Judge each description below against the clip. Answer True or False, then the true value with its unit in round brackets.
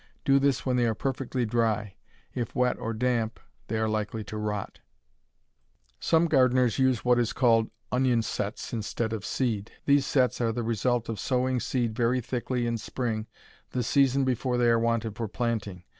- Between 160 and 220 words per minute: True (175 wpm)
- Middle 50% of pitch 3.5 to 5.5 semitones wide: False (2.4 semitones)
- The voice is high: False (120 Hz)